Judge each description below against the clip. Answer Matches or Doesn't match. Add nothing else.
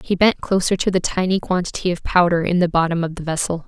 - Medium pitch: Matches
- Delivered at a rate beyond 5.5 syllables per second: Matches